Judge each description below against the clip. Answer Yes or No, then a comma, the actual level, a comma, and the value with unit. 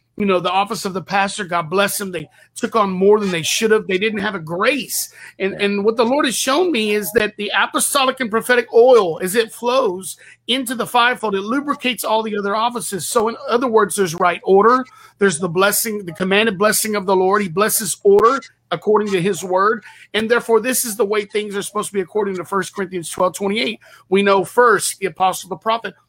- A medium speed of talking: No, fast, 225 wpm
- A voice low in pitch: No, high, 210 Hz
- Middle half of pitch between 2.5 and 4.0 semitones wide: Yes, average, 3.1 semitones